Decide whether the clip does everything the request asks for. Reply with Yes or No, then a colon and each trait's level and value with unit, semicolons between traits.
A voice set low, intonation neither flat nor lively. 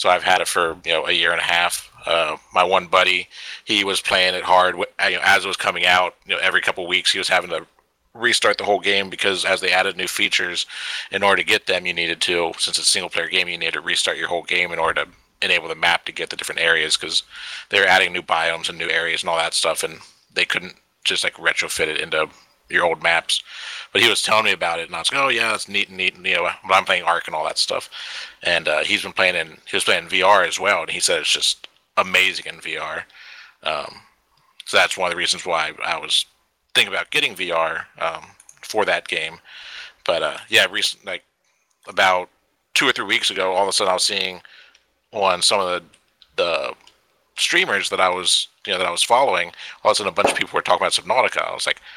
No: very low, 90 Hz; narrow, 2.0 semitones